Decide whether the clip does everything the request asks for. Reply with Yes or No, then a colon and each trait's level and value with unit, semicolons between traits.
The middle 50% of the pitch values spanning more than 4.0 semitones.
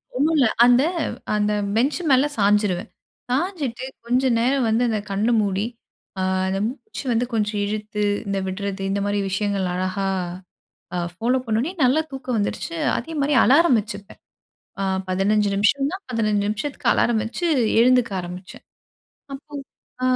Yes: average, 4.4 semitones